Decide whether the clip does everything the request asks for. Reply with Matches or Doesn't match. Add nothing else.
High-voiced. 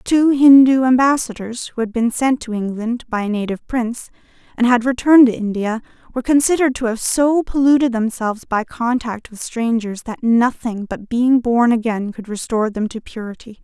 Matches